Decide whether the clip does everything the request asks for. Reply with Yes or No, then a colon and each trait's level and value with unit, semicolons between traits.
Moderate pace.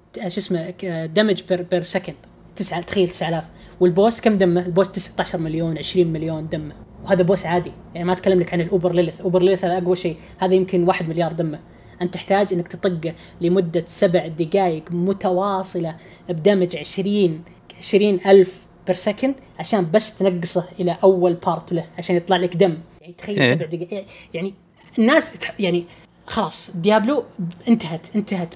No: fast, 160 wpm